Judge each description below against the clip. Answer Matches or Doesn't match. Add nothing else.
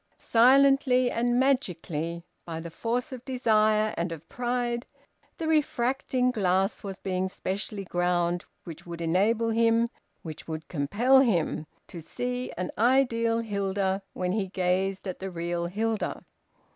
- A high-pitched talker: Matches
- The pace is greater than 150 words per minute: Doesn't match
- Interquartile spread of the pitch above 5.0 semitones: Matches